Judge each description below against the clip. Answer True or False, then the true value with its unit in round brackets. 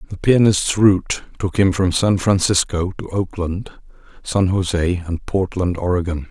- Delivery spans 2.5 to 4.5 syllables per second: True (4.3 syllables/s)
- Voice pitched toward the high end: False (95 Hz)